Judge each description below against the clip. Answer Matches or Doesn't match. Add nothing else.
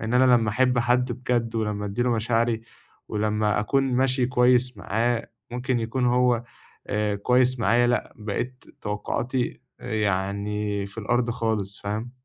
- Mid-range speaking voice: Doesn't match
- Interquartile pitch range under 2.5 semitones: Doesn't match